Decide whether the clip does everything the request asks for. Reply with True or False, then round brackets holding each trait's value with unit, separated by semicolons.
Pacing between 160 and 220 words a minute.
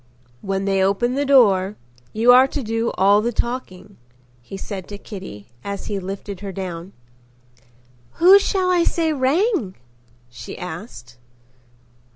False (140 wpm)